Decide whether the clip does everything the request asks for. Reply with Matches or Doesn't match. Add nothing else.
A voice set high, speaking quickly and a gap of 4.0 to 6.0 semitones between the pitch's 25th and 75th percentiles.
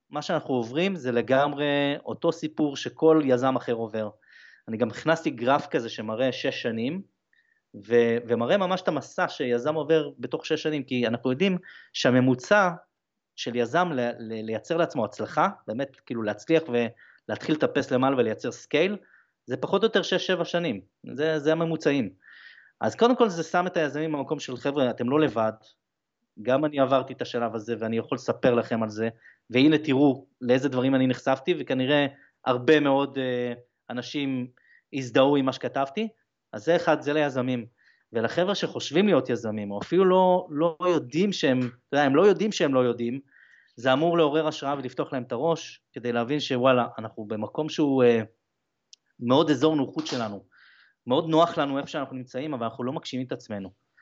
Doesn't match